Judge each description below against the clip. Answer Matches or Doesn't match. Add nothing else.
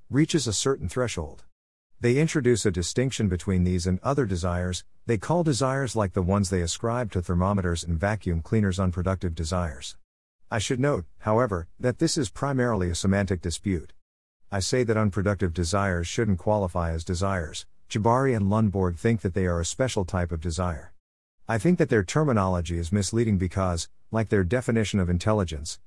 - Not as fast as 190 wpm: Matches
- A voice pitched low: Matches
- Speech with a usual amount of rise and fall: Matches